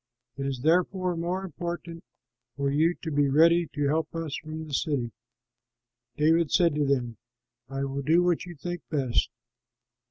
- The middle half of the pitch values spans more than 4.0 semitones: No, average, 3.5 semitones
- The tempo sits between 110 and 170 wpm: Yes, average, 160 wpm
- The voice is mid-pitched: Yes, medium, 155 Hz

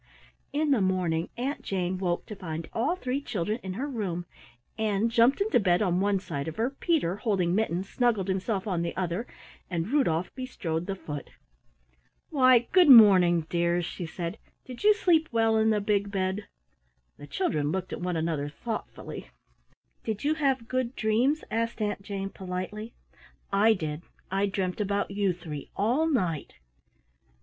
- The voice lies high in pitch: Yes, high, 200 Hz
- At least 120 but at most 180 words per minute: Yes, average, 165 wpm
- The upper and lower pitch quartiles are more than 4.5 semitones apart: Yes, average, 5.0 semitones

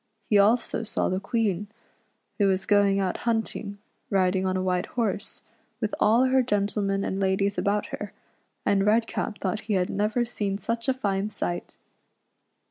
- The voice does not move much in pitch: Yes, narrow, 2.3 semitones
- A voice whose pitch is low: No, high, 205 Hz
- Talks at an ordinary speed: Yes, average, 165 wpm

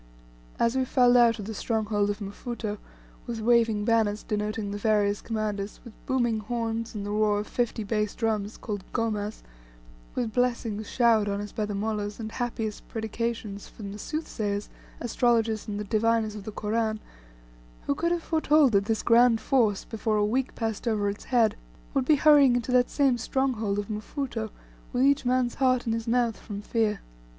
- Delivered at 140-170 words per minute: No, average, 180 wpm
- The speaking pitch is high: Yes, high, 225 Hz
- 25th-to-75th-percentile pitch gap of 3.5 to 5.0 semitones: No, narrow, 2.5 semitones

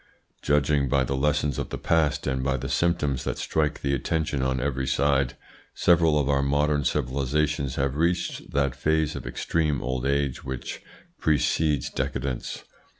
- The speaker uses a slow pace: No, average, 155 wpm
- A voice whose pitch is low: Yes, very low, 70 Hz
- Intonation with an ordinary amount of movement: No, narrow, 2.2 semitones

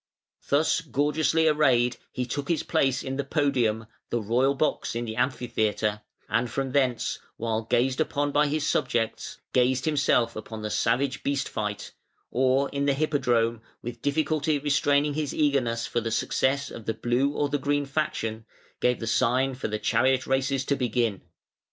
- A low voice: Yes, low, 130 Hz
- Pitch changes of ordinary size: Yes, average, 3.5 semitones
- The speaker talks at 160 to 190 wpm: Yes, average, 165 wpm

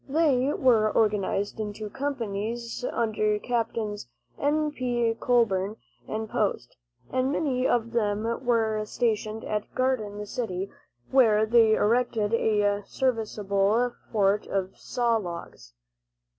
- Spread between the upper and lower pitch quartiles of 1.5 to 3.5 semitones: Yes, average, 2.8 semitones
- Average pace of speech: No, slow, 110 wpm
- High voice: Yes, high, 220 Hz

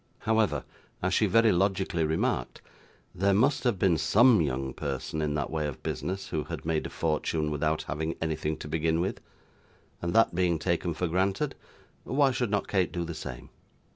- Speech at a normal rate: Yes, average, 180 wpm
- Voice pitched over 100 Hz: No, very low, 85 Hz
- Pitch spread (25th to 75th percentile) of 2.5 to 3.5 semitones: No, average, 4.1 semitones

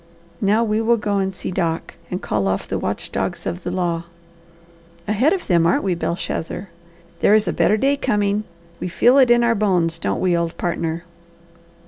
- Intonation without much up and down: No, average, 4.2 semitones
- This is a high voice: Yes, high, 195 Hz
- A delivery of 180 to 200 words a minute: Yes, average, 190 wpm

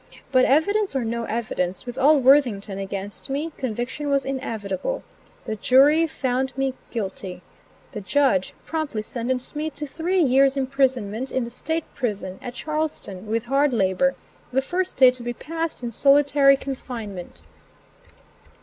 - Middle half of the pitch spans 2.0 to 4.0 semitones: No, average, 4.4 semitones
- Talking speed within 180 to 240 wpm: No, average, 145 wpm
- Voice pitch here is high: Yes, very high, 260 Hz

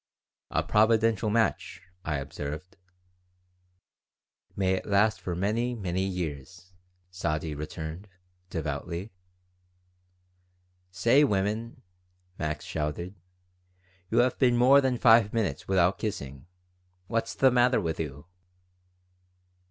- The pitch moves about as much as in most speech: No, wide, 5.9 semitones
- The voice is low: Yes, very low, 95 Hz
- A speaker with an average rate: No, slow, 100 wpm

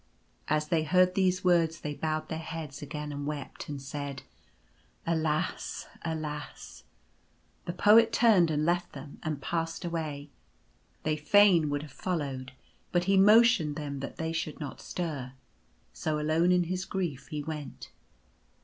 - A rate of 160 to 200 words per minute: No, average, 150 wpm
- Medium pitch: Yes, medium, 155 Hz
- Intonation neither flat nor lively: Yes, average, 3.1 semitones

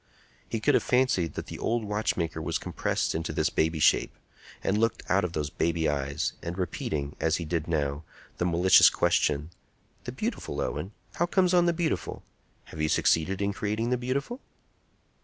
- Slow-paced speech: No, average, 175 wpm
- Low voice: Yes, very low, 90 Hz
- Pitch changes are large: Yes, wide, 6.5 semitones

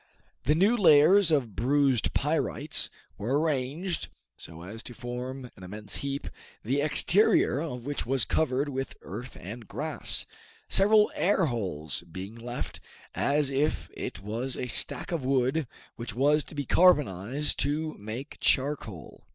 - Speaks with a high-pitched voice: No, low, 135 Hz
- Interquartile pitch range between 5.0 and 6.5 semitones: No, average, 4.3 semitones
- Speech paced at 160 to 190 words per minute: No, average, 145 wpm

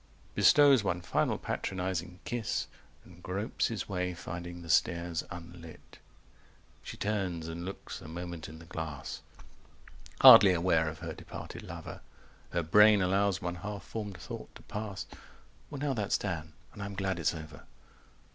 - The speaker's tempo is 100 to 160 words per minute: Yes, average, 155 wpm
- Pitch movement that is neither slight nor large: Yes, average, 3.2 semitones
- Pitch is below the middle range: Yes, very low, 90 Hz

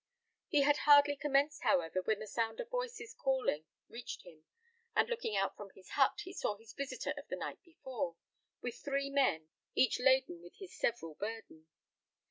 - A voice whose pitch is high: Yes, very high, 260 Hz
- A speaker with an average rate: Yes, average, 175 wpm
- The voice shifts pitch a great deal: Yes, wide, 6.7 semitones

